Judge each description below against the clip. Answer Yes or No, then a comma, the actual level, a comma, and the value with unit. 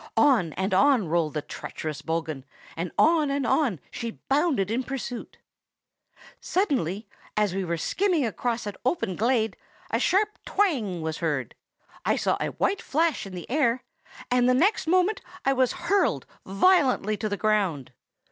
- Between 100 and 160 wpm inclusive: Yes, average, 155 wpm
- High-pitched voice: Yes, high, 235 Hz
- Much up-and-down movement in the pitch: Yes, wide, 8.2 semitones